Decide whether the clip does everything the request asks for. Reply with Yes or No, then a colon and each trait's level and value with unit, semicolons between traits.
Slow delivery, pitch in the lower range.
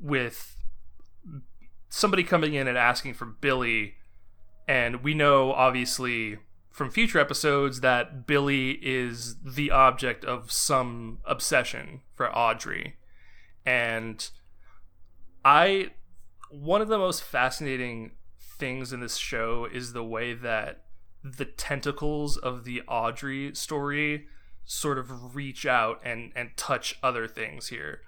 Yes: slow, 120 wpm; low, 125 Hz